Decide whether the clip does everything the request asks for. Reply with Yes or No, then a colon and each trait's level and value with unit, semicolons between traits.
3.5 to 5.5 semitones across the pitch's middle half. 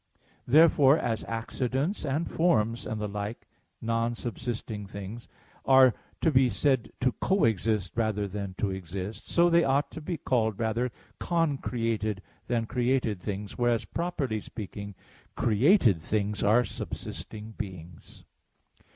Yes: average, 4.2 semitones